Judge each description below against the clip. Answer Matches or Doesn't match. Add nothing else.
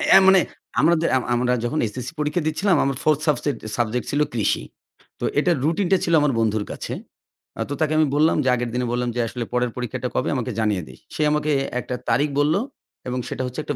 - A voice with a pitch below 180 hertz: Matches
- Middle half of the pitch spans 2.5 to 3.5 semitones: Doesn't match